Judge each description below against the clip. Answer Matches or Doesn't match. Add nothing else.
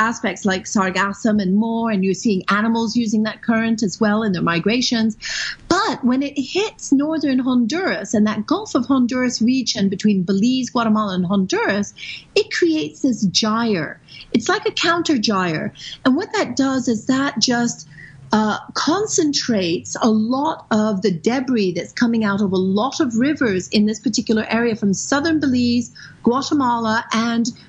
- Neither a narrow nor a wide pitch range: Matches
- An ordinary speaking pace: Matches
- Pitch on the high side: Matches